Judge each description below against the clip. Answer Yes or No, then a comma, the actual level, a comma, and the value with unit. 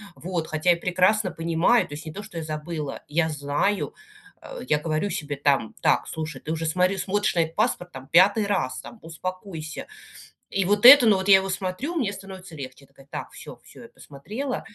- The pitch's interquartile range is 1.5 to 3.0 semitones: No, average, 4.4 semitones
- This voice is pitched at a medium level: Yes, medium, 175 Hz